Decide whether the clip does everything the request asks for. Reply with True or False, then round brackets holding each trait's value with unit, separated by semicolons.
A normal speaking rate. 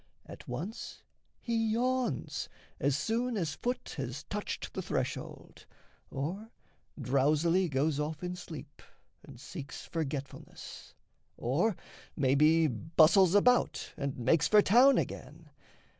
False (115 wpm)